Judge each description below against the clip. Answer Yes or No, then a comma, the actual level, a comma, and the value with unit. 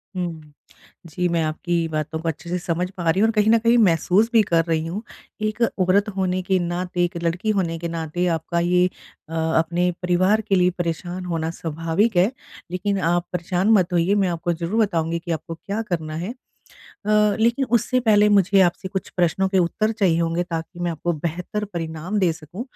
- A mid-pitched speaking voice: Yes, medium, 175 Hz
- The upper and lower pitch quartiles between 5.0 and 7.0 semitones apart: No, average, 3.1 semitones